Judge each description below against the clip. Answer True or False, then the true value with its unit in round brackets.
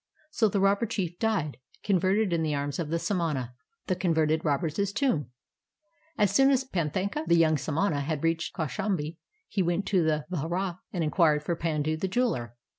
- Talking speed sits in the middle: True (175 wpm)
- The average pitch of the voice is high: False (170 Hz)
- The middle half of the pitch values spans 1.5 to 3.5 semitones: False (4.3 semitones)